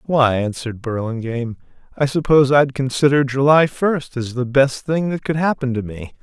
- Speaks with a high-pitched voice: No, low, 135 Hz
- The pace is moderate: Yes, average, 175 wpm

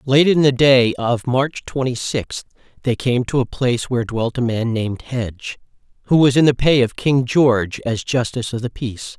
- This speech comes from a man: Yes, male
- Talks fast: Yes, fast, 210 wpm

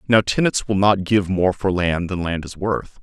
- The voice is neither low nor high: No, very low, 95 Hz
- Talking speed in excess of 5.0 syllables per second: No, 4.6 syllables/s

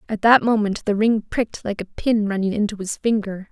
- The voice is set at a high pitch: Yes, high, 210 Hz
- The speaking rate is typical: No, fast, 220 wpm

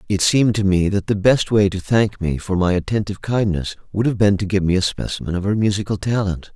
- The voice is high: No, low, 100 Hz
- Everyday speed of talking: No, fast, 245 wpm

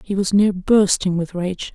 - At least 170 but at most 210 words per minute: Yes, fast, 205 wpm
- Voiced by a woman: Yes, female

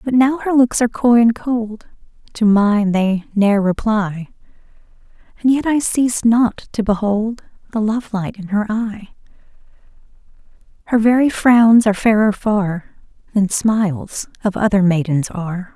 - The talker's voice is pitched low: No, high, 215 Hz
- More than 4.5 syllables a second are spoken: No, 4.4 syllables/s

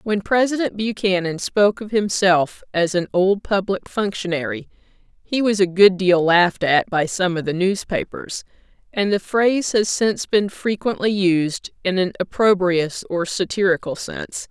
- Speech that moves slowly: No, average, 155 wpm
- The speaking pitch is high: Yes, high, 195 Hz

